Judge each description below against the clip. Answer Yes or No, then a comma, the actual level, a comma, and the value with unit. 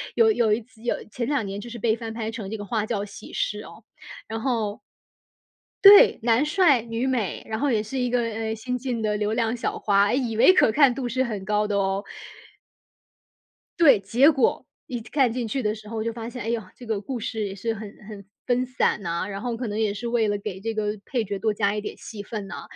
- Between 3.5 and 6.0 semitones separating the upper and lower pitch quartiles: No, average, 2.7 semitones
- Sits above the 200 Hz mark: Yes, high, 225 Hz